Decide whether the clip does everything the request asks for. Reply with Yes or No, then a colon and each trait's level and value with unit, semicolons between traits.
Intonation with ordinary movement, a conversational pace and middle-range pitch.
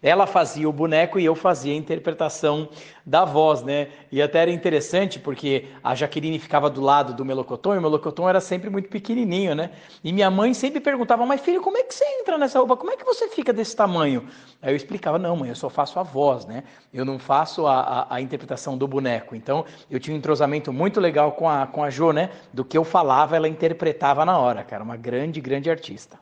No: average, 5.0 semitones; fast, 225 wpm; medium, 155 Hz